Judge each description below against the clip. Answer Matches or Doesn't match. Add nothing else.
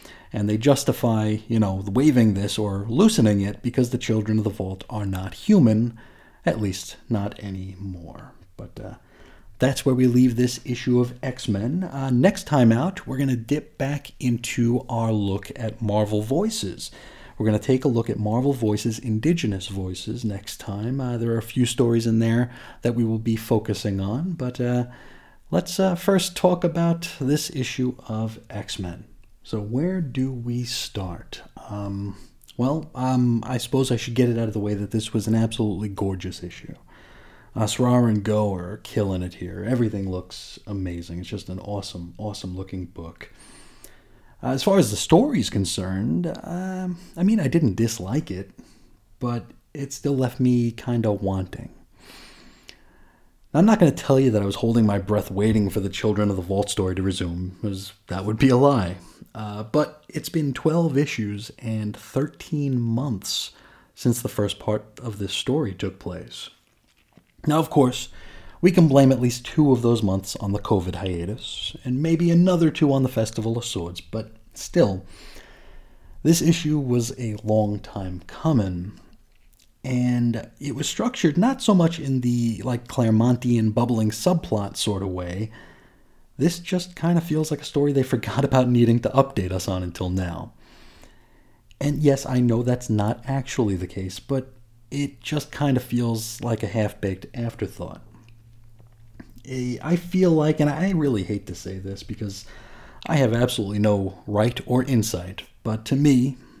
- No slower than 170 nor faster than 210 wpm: Matches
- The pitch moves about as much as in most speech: Matches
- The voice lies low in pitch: Matches